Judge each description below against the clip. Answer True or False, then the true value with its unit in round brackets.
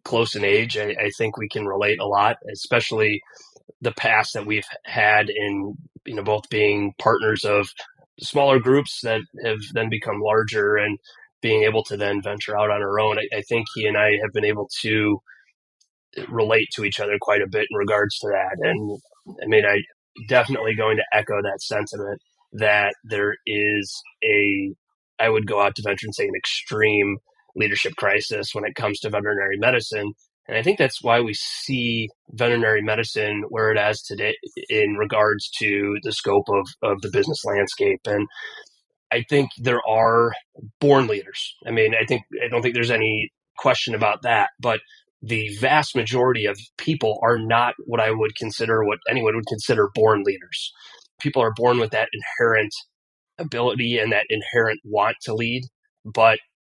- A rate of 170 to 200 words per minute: True (180 wpm)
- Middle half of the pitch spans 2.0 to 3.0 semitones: True (2.7 semitones)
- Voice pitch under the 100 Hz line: False (110 Hz)